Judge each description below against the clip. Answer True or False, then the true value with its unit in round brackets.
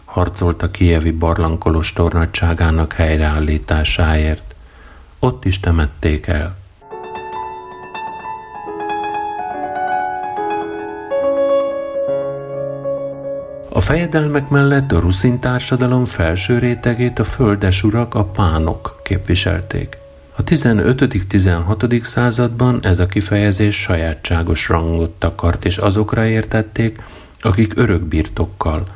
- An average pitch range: False (8.2 semitones)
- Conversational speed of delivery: False (80 wpm)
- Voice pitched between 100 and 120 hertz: True (105 Hz)